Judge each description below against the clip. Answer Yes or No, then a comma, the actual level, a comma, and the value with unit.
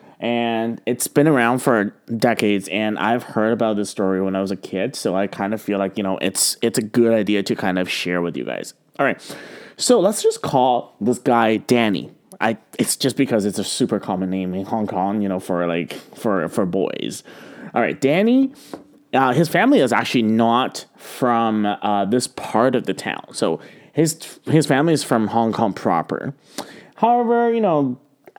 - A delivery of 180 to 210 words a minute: Yes, average, 195 wpm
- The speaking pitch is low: Yes, low, 115 Hz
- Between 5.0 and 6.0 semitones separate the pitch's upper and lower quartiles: Yes, average, 5.3 semitones